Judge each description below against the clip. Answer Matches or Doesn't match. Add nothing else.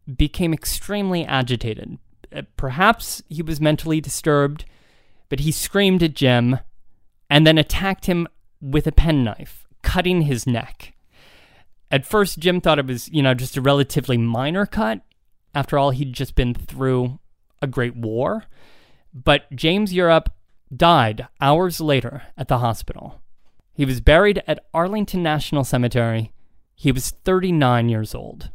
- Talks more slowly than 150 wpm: Matches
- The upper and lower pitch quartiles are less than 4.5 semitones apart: Doesn't match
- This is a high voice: Doesn't match